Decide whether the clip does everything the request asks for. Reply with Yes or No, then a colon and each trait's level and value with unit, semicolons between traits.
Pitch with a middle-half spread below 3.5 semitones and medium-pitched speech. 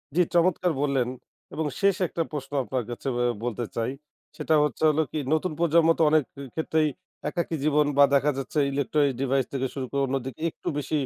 Yes: average, 3.1 semitones; medium, 145 Hz